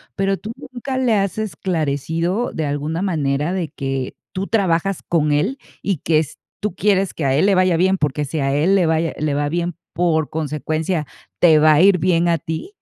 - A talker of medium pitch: Yes, medium, 165 Hz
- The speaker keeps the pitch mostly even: No, average, 4.1 semitones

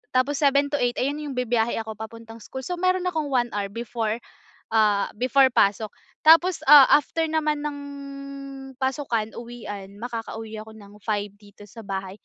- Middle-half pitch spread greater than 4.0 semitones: Yes, average, 4.8 semitones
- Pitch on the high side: Yes, high, 235 Hz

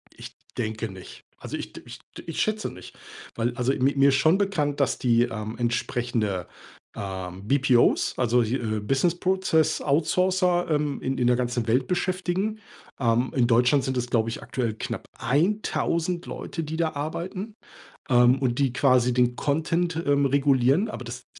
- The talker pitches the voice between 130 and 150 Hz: Yes, low, 135 Hz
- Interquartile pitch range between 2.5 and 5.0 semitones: No, wide, 5.4 semitones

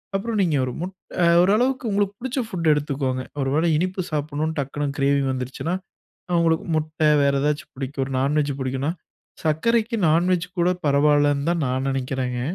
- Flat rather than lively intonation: No, average, 4.4 semitones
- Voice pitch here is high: No, medium, 150 Hz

